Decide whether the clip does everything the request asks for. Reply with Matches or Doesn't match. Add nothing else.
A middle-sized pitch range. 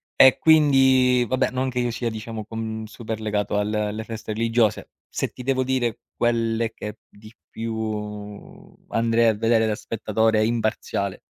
Doesn't match